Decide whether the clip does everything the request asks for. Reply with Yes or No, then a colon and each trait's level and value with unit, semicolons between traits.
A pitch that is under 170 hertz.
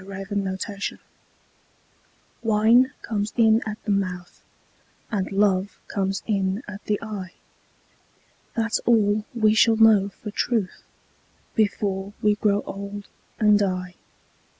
No: high, 205 Hz